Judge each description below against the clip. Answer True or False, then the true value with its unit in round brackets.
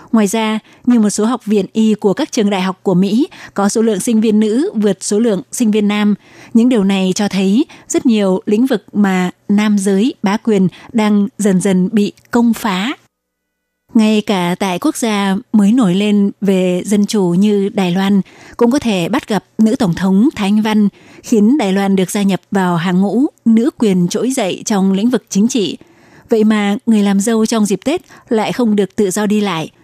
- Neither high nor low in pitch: False (210 Hz)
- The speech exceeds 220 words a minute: False (210 wpm)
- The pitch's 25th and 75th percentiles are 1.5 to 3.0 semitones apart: True (2.6 semitones)